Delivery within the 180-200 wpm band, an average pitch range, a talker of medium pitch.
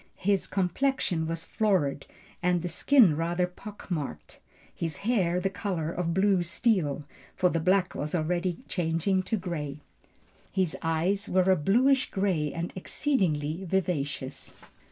No: slow, 135 wpm; average, 3.2 semitones; medium, 180 Hz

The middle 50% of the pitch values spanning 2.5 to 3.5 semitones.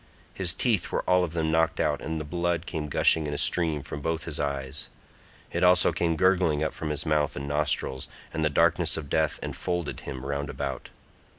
Yes: average, 2.8 semitones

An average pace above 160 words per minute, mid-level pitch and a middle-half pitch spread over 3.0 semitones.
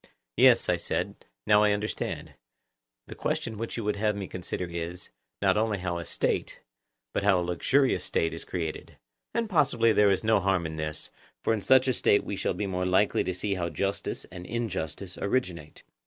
No: average, 195 wpm; low, 100 Hz; average, 3.7 semitones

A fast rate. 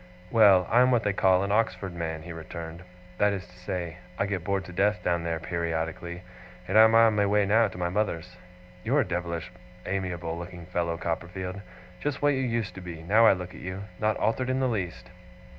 Yes: fast, 215 wpm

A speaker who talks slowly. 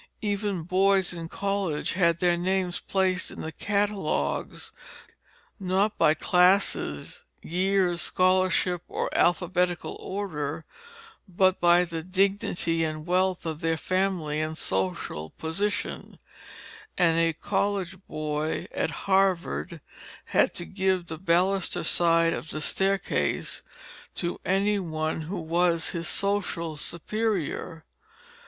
Yes: slow, 115 wpm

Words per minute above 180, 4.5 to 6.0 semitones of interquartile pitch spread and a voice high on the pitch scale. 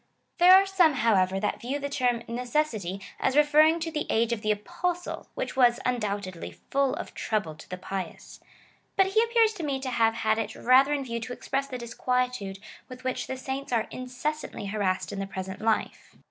Yes: average, 200 wpm; average, 5.1 semitones; very high, 250 Hz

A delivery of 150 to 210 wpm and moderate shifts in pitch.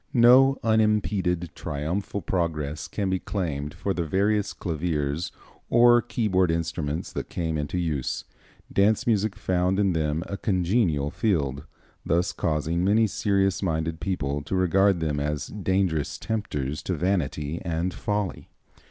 No: slow, 135 wpm; average, 4.5 semitones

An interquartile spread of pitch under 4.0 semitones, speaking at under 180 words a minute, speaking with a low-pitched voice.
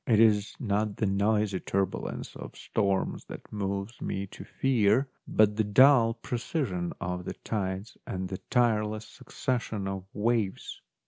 Yes: average, 2.7 semitones; average, 140 wpm; low, 105 Hz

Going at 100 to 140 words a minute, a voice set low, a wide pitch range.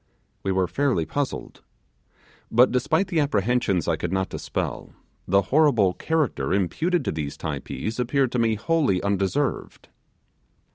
Yes: slow, 135 wpm; low, 115 Hz; wide, 7.2 semitones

